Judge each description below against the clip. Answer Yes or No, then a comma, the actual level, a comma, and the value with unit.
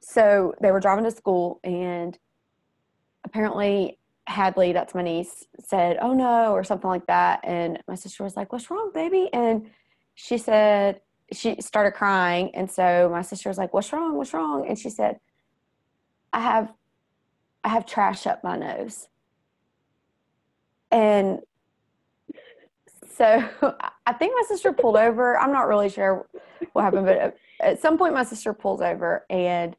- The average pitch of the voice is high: Yes, high, 205 Hz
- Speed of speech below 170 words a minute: Yes, average, 155 wpm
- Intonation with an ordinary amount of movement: Yes, average, 4.2 semitones